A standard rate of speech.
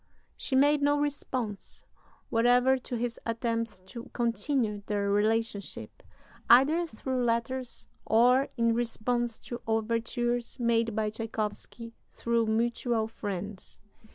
No: slow, 110 wpm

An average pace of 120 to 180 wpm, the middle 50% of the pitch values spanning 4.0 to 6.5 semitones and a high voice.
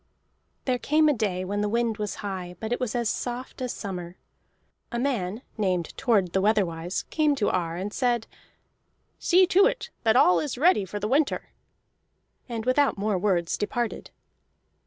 Yes: average, 170 wpm; average, 4.9 semitones; high, 215 Hz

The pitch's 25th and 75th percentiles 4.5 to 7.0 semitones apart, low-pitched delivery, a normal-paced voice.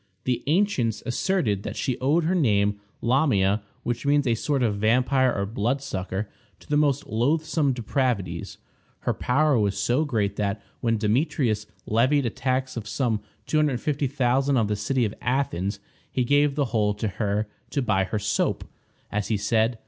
Yes: average, 4.8 semitones; low, 120 Hz; average, 165 wpm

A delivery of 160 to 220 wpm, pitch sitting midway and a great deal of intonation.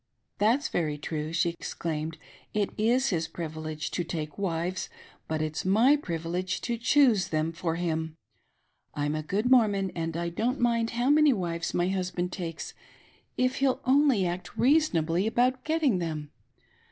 Yes: average, 165 wpm; medium, 180 Hz; wide, 6.6 semitones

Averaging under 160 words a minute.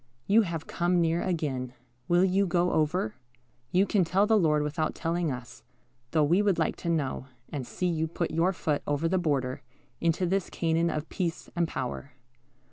No: average, 185 wpm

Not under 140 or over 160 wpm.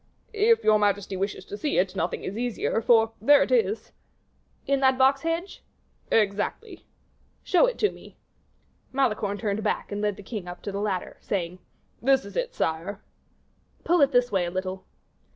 No: average, 175 wpm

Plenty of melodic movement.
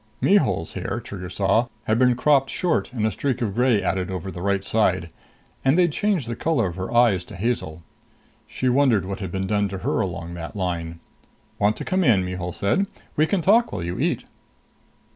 Yes: wide, 5.8 semitones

